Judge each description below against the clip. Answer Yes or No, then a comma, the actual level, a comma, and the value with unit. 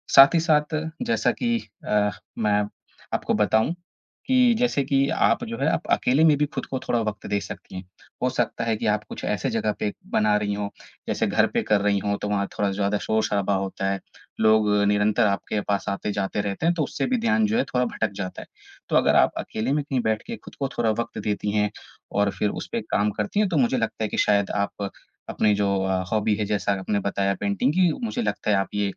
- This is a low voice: Yes, low, 105 Hz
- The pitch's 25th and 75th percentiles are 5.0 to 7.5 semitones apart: Yes, average, 5.3 semitones